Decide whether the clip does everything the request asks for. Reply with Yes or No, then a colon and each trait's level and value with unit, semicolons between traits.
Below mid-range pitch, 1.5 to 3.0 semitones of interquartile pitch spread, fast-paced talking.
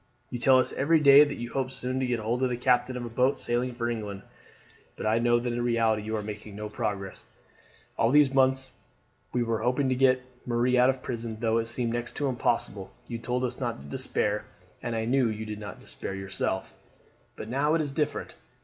Yes: low, 120 Hz; narrow, 2.6 semitones; fast, 225 wpm